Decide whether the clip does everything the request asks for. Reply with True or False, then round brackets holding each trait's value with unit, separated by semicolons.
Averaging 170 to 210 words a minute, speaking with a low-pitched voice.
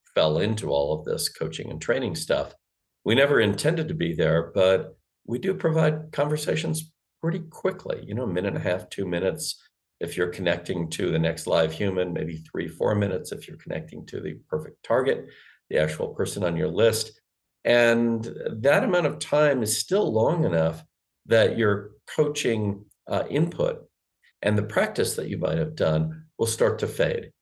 True (180 wpm; 105 Hz)